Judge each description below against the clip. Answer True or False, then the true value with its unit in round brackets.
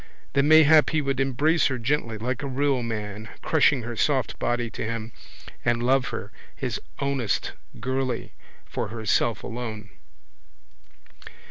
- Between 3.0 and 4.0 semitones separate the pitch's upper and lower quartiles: True (3.4 semitones)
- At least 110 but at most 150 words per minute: True (135 wpm)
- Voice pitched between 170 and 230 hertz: False (125 Hz)